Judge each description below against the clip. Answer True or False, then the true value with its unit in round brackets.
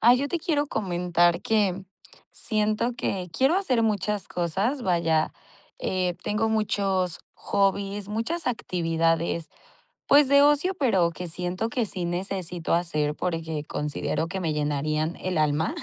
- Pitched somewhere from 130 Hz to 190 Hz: True (185 Hz)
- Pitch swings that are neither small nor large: True (4.9 semitones)